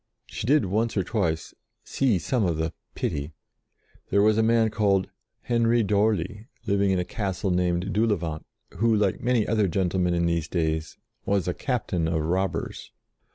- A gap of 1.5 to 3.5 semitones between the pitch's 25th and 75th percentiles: No, average, 4.1 semitones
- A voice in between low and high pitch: No, very low, 95 Hz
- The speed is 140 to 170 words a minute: Yes, average, 160 wpm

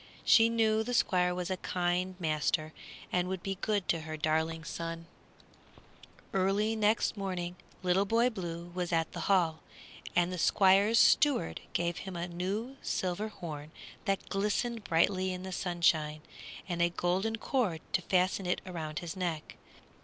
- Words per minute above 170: No, average, 160 wpm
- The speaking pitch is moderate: Yes, medium, 180 Hz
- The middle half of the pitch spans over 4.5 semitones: No, average, 2.7 semitones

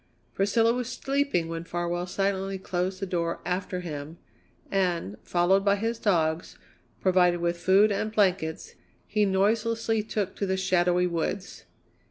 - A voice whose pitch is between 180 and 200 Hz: Yes, high, 190 Hz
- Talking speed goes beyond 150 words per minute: No, average, 140 wpm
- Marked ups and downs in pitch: No, narrow, 2.6 semitones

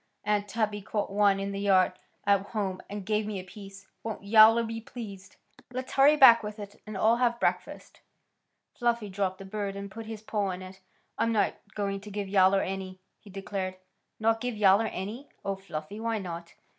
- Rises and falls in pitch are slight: Yes, narrow, 2.3 semitones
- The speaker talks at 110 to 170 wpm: No, average, 200 wpm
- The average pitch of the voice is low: No, high, 205 Hz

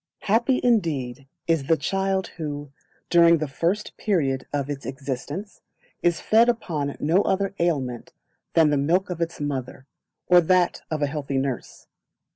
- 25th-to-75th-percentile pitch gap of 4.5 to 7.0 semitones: Yes, average, 4.8 semitones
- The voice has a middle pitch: Yes, medium, 160 Hz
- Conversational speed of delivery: Yes, average, 150 wpm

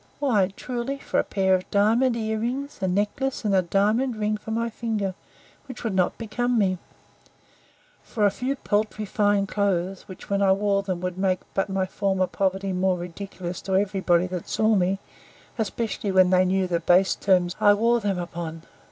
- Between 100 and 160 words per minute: No, average, 185 wpm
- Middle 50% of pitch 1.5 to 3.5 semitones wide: Yes, average, 2.7 semitones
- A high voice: Yes, high, 200 Hz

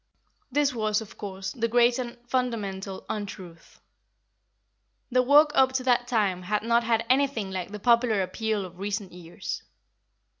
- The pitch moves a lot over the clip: No, average, 4.0 semitones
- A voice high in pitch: Yes, high, 220 Hz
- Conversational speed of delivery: Yes, average, 150 wpm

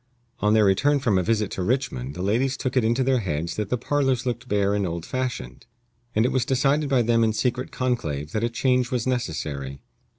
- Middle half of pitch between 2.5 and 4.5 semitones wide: No, average, 5.0 semitones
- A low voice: Yes, low, 115 Hz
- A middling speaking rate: No, fast, 220 wpm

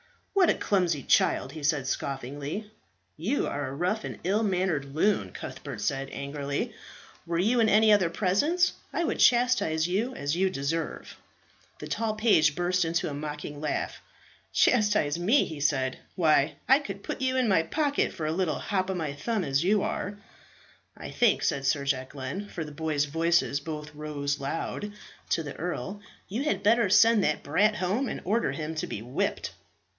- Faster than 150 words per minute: Yes, average, 180 wpm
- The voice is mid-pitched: Yes, medium, 170 Hz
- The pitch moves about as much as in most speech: No, wide, 6.3 semitones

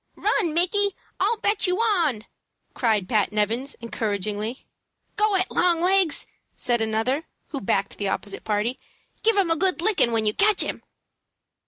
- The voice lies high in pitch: Yes, very high, 280 Hz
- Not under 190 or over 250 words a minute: No, average, 155 wpm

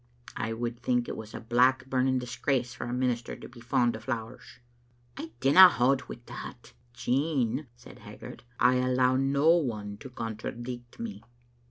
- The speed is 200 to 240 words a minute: No, average, 175 wpm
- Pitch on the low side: Yes, low, 125 Hz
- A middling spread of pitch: No, narrow, 1.6 semitones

